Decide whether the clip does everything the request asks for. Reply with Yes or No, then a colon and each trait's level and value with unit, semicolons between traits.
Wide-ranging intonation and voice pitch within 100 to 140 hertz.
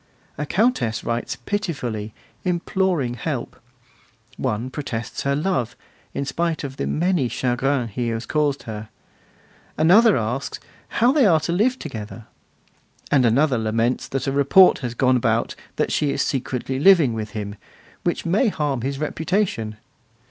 Yes: wide, 6.3 semitones; low, 135 Hz